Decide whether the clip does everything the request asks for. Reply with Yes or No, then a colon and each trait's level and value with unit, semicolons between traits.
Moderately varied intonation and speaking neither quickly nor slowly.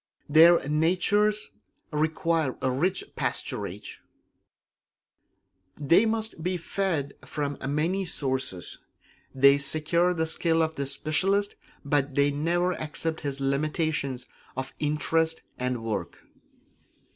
No: average, 3.6 semitones; slow, 100 wpm